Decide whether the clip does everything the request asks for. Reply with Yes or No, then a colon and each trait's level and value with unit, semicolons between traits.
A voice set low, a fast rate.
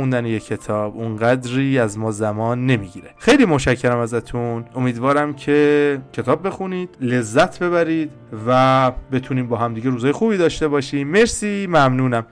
No: low, 130 Hz; average, 130 wpm